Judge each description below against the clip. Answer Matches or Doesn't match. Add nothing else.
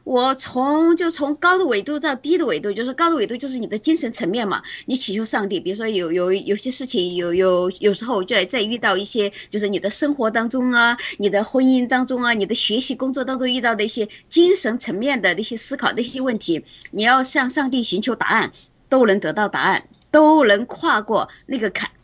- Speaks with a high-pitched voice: Matches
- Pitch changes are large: Doesn't match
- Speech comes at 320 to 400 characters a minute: Matches